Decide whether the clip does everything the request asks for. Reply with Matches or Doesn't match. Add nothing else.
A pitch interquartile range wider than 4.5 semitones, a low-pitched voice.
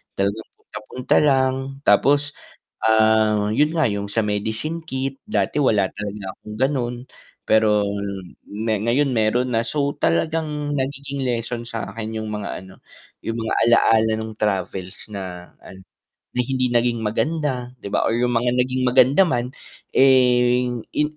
Doesn't match